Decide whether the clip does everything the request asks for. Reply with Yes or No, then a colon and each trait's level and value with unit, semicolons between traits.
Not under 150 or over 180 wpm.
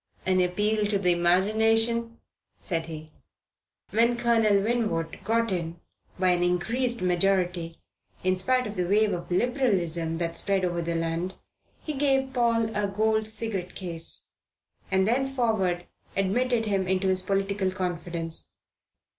No: slow, 135 wpm